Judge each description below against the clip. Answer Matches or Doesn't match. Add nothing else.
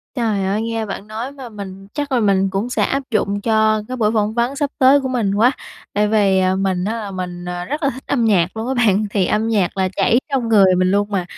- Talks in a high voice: Matches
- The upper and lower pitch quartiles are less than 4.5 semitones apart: Matches